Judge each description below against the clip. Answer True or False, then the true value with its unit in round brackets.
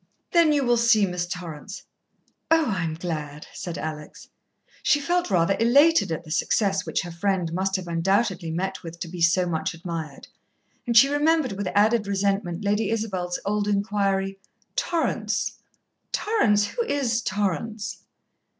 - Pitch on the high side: True (195 Hz)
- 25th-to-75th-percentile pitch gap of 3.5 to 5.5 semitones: True (4.7 semitones)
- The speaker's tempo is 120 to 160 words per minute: True (150 wpm)